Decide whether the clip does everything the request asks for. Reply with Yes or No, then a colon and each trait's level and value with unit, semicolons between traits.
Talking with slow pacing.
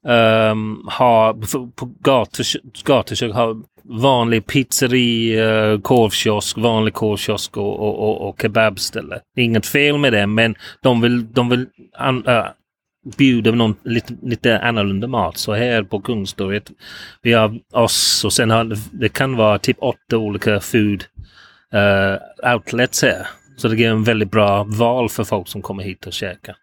No: average, 160 wpm